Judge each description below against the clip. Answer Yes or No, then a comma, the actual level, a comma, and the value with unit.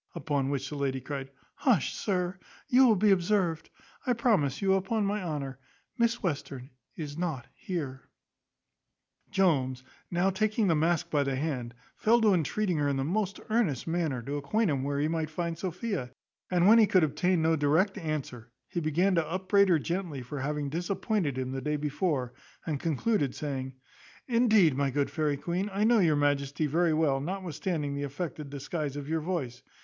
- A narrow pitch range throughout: No, average, 5.1 semitones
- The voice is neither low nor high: Yes, medium, 160 Hz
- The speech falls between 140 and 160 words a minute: No, average, 180 wpm